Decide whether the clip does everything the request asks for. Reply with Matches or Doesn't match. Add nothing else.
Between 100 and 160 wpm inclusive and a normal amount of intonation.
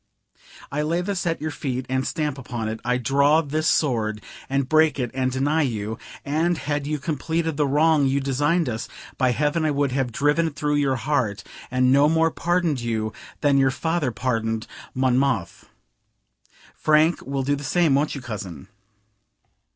Doesn't match